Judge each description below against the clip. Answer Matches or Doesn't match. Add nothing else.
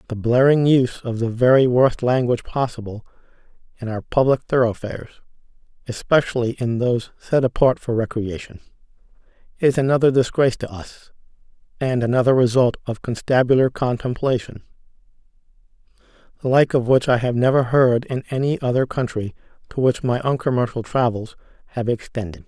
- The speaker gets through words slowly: Matches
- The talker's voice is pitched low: Matches